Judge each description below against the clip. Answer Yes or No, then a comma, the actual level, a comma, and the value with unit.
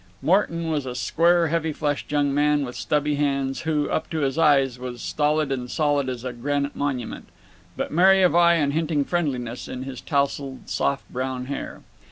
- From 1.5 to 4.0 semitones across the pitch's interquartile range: Yes, average, 2.8 semitones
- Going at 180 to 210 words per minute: Yes, average, 185 wpm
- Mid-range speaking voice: Yes, medium, 145 Hz